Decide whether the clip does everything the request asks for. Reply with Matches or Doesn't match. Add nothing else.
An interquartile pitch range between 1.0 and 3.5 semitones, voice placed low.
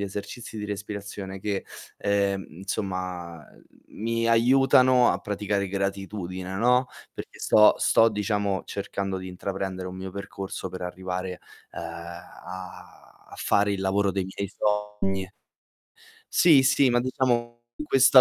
Matches